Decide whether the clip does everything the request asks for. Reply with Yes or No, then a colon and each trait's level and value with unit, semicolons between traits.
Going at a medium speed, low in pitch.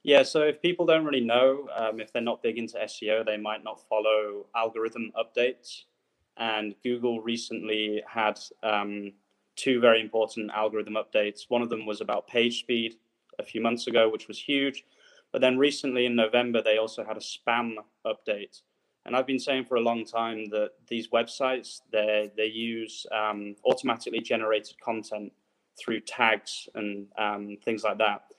Yes: average, 165 wpm; low, 115 Hz